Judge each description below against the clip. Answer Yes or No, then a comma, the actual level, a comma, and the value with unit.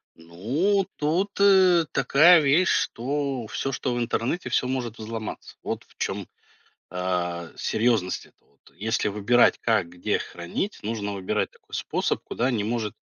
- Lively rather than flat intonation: Yes, wide, 6.2 semitones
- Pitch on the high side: No, low, 120 Hz